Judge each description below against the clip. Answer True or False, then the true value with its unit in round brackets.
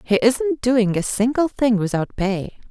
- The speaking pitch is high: True (230 Hz)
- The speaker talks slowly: False (175 wpm)